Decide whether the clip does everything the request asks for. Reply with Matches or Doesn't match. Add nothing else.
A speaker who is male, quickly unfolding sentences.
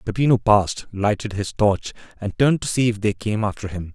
Matches